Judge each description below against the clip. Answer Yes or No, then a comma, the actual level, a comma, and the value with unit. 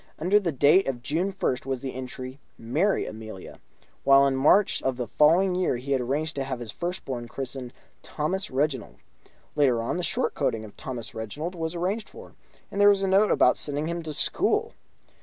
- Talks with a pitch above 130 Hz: Yes, medium, 140 Hz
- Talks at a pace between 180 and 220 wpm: Yes, average, 195 wpm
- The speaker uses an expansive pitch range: Yes, wide, 5.7 semitones